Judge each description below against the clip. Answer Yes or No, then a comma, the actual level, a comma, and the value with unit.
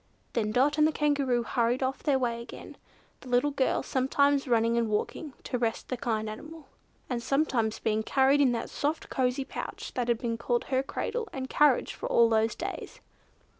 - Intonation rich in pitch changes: No, average, 3.3 semitones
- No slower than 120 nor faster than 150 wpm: No, average, 185 wpm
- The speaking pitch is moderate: No, very high, 255 Hz